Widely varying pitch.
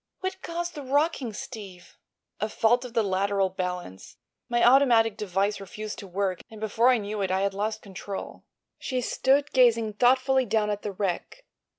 No: average, 4.2 semitones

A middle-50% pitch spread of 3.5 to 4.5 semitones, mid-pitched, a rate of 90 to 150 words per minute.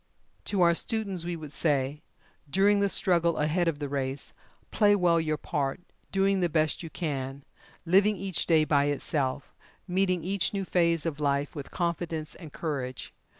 No: average, 4.1 semitones; medium, 165 Hz; average, 165 wpm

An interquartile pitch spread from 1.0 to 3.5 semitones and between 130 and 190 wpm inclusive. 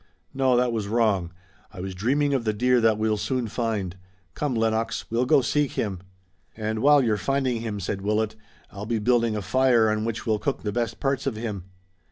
No: average, 2.9 semitones; fast, 205 wpm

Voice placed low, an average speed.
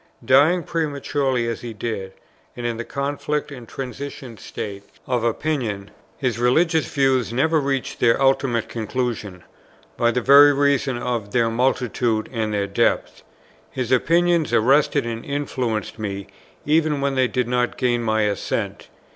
Yes: low, 125 Hz; average, 145 wpm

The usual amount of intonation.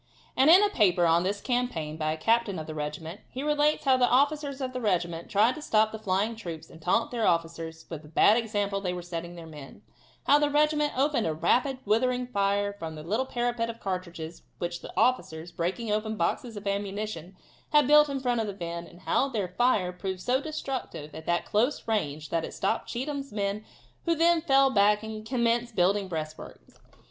No: wide, 6.6 semitones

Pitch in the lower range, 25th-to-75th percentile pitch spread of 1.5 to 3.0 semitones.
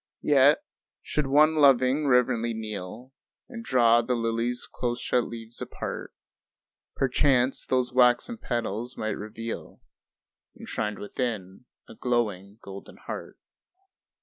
Yes: low, 120 Hz; narrow, 2.6 semitones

